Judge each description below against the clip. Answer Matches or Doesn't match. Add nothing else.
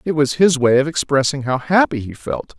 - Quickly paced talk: Matches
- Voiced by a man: Matches